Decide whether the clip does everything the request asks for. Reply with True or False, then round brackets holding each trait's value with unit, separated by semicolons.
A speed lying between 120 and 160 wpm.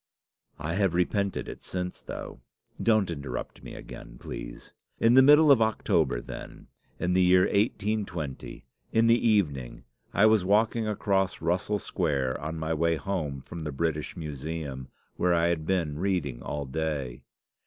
True (155 wpm)